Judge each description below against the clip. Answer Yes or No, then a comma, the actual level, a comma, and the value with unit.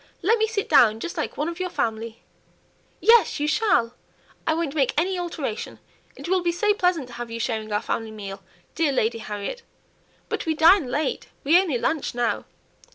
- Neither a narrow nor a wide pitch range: No, wide, 7.4 semitones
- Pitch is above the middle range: Yes, very high, 305 Hz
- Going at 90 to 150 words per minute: No, average, 190 wpm